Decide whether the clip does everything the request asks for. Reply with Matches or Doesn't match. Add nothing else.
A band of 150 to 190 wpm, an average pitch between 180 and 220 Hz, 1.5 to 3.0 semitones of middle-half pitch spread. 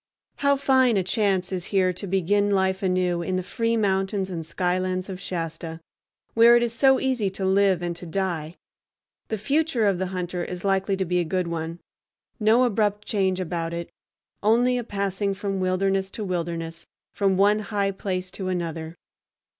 Matches